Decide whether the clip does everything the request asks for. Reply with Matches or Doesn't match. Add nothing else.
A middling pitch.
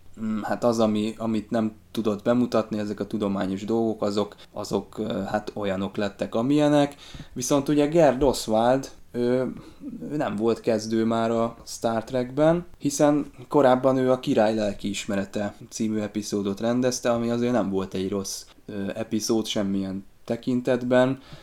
Doesn't match